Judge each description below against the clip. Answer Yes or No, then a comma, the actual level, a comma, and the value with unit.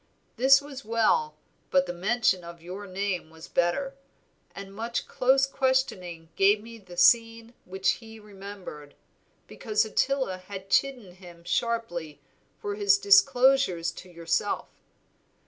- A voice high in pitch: Yes, high, 200 Hz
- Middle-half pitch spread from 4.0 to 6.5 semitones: Yes, average, 4.6 semitones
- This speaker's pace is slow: Yes, slow, 130 wpm